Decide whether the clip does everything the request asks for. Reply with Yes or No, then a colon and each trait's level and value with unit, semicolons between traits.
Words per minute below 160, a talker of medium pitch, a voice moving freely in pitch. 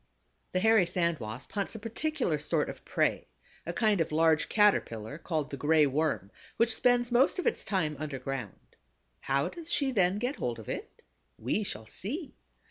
No: average, 175 wpm; medium, 170 Hz; wide, 7.8 semitones